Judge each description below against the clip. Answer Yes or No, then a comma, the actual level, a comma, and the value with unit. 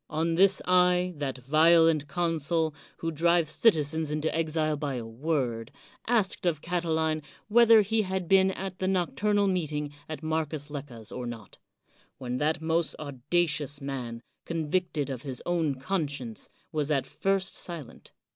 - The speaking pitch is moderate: Yes, medium, 160 Hz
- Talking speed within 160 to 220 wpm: No, average, 145 wpm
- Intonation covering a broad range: No, average, 3.7 semitones